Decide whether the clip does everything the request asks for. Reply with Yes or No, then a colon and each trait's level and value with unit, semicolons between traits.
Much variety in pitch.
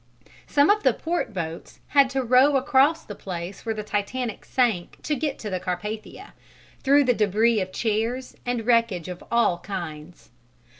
Yes: wide, 5.7 semitones